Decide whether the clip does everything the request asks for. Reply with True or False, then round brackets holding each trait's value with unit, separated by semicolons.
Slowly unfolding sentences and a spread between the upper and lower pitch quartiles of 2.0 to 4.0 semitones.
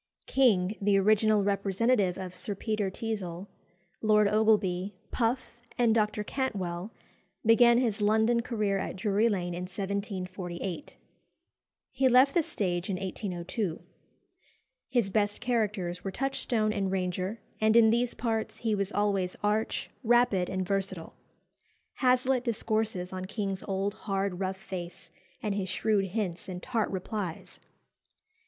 True (130 wpm; 3.0 semitones)